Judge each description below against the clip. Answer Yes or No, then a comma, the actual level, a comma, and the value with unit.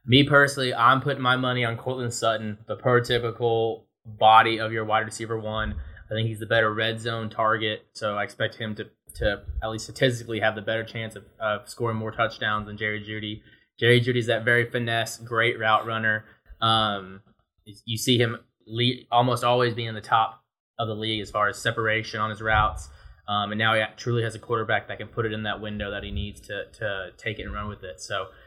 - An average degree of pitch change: No, narrow, 1.6 semitones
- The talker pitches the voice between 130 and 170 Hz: No, low, 110 Hz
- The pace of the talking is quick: Yes, fast, 215 wpm